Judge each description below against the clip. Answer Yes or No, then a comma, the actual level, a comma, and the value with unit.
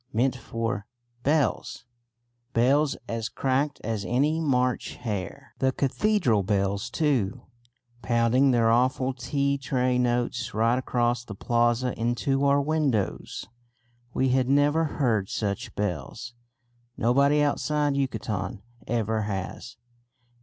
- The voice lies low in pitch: Yes, low, 125 Hz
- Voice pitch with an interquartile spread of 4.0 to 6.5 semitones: No, average, 3.4 semitones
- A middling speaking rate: No, slow, 110 wpm